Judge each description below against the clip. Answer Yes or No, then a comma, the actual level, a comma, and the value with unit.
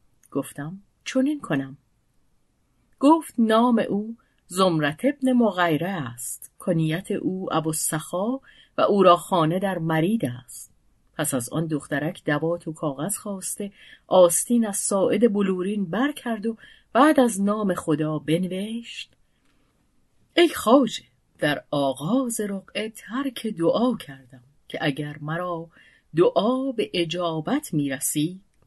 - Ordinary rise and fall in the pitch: No, wide, 6.5 semitones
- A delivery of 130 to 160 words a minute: No, average, 120 wpm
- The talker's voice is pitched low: No, medium, 180 Hz